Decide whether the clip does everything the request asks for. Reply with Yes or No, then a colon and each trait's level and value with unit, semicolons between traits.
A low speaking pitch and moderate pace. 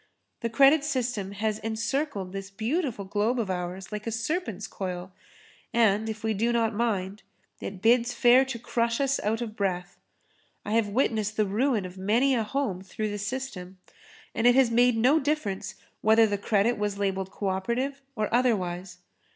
No: high, 220 Hz; average, 175 wpm